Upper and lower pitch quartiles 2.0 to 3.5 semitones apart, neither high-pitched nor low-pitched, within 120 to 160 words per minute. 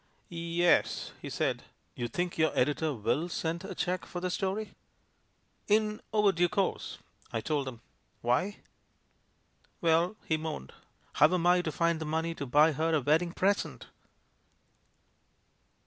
Yes: average, 2.8 semitones; medium, 165 Hz; average, 150 wpm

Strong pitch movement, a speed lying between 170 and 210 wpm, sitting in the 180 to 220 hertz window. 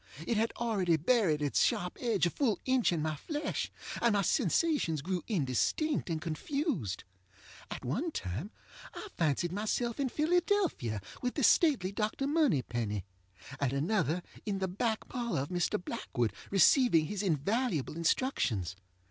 No: wide, 8.3 semitones; average, 145 wpm; high, 190 Hz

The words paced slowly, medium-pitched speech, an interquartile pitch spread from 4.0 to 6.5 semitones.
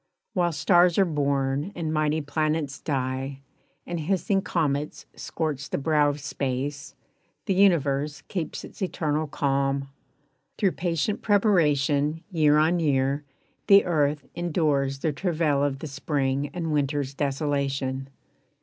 No: slow, 125 wpm; medium, 150 Hz; average, 3.1 semitones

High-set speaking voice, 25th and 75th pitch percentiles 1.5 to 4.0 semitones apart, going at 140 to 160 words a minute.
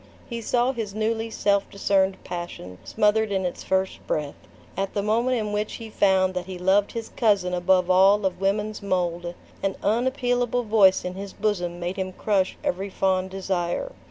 No: high, 195 Hz; narrow, 2.6 semitones; average, 175 wpm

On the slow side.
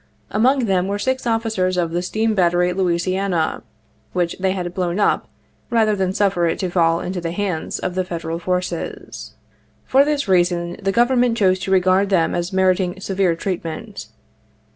No: average, 170 wpm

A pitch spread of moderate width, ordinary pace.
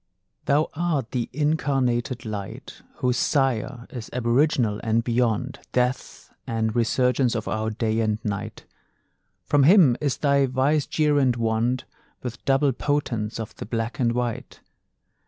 No: average, 3.4 semitones; slow, 130 wpm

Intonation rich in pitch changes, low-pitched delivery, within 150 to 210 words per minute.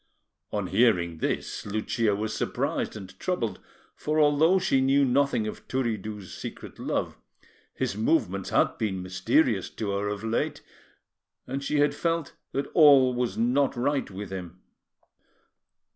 No: wide, 5.9 semitones; low, 115 Hz; average, 140 wpm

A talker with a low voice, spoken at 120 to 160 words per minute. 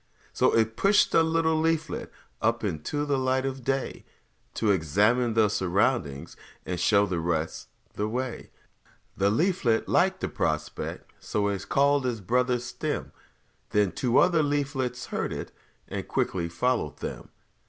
Yes: low, 120 Hz; average, 145 wpm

